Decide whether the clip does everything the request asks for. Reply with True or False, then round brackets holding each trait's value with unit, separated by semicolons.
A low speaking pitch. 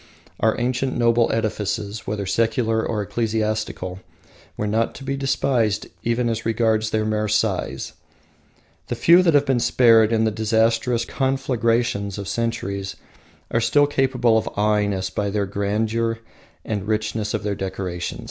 True (110 Hz)